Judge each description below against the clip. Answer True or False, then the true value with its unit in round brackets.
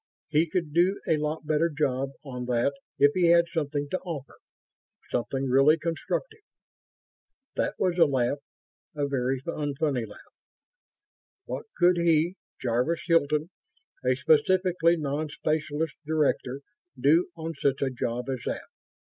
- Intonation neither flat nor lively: True (3.5 semitones)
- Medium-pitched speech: True (150 Hz)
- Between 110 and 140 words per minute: True (135 wpm)